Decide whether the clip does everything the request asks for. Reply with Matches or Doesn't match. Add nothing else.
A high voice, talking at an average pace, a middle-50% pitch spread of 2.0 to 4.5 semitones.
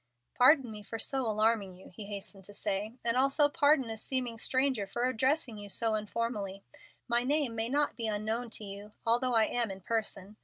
Matches